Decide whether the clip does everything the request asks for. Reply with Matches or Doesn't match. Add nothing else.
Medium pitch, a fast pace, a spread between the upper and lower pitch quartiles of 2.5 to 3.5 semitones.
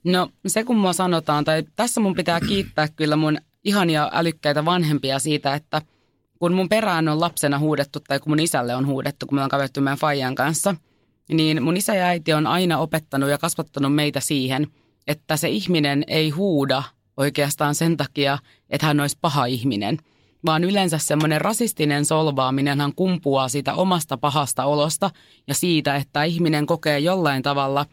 Matches